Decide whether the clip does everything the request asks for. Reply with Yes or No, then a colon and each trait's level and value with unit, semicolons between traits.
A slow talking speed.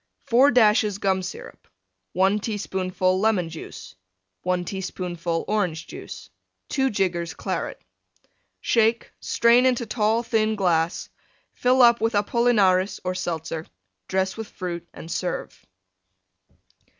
Yes: slow, 115 wpm